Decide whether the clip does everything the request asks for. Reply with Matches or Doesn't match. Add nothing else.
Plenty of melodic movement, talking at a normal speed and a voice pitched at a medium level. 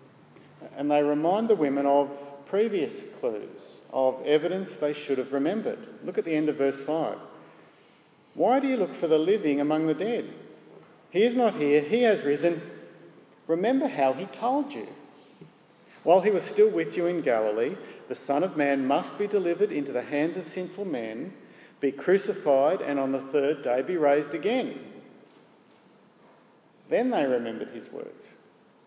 Matches